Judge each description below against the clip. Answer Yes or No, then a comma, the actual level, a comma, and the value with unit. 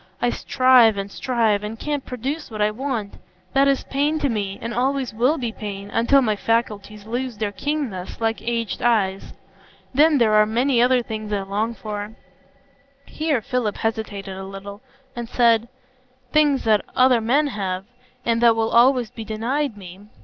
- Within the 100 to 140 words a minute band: No, average, 165 wpm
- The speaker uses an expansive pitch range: No, average, 3.6 semitones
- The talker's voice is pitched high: Yes, high, 230 Hz